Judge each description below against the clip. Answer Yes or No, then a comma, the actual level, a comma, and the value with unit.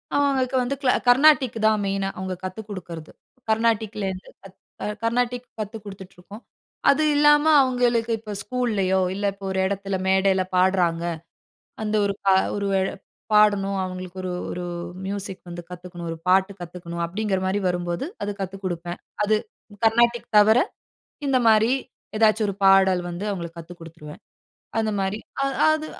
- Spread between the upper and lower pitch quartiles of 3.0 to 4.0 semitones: Yes, average, 3.5 semitones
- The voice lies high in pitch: Yes, high, 200 Hz